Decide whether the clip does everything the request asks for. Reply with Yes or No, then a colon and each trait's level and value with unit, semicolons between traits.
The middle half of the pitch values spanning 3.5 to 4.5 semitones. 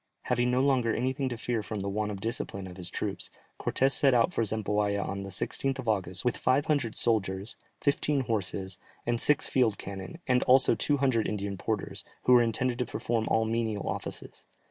Yes: average, 4.0 semitones